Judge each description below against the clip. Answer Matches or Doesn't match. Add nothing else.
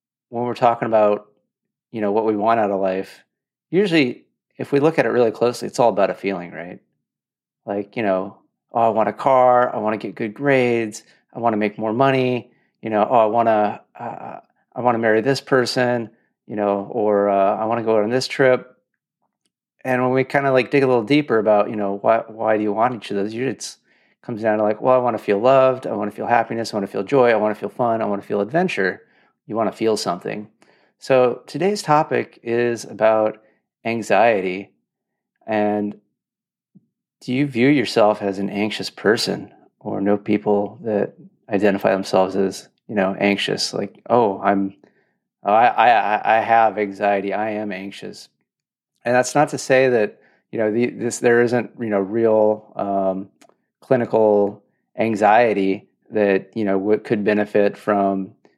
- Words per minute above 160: Matches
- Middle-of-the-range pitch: Doesn't match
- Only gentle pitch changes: Doesn't match